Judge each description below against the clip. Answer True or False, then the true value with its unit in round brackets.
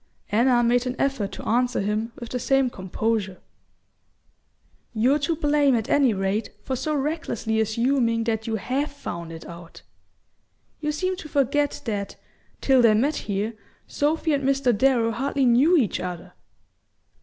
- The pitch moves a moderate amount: True (4.2 semitones)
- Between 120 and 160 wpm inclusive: True (155 wpm)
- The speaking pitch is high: True (245 Hz)